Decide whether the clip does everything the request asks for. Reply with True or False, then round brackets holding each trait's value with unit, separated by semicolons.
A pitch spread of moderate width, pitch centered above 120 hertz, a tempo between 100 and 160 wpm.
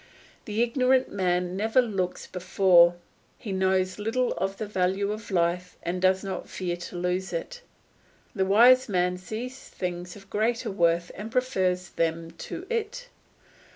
True (3.6 semitones; 190 Hz; 150 wpm)